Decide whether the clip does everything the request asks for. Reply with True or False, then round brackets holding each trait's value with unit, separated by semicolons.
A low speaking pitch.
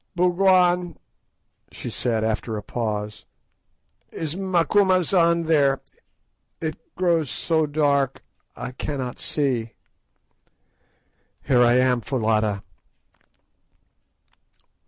False (145 Hz)